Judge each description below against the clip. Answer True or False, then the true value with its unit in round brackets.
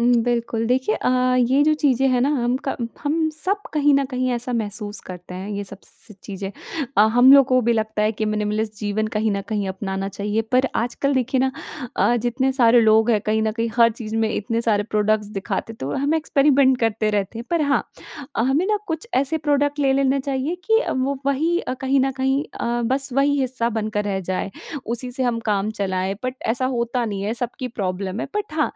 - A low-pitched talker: False (240 Hz)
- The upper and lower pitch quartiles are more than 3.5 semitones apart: True (4.1 semitones)